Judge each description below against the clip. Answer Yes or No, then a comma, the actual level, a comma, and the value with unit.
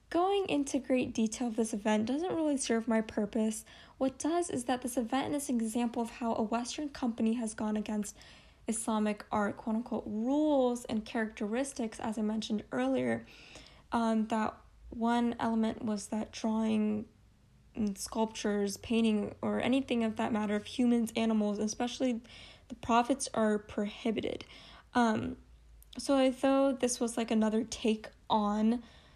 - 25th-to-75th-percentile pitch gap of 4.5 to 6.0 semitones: No, narrow, 2.6 semitones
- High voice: Yes, high, 230 Hz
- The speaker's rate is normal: Yes, average, 150 wpm